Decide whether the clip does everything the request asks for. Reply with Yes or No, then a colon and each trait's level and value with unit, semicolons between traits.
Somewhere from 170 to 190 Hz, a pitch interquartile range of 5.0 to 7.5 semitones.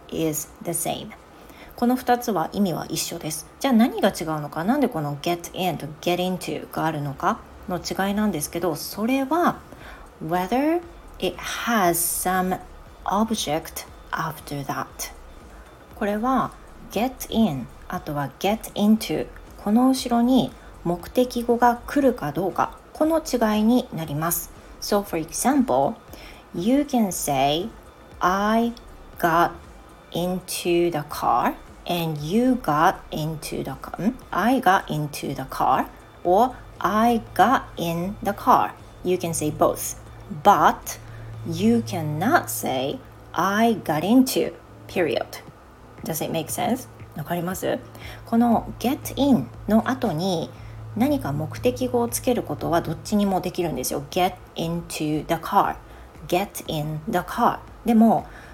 Yes: medium, 185 Hz; wide, 6.5 semitones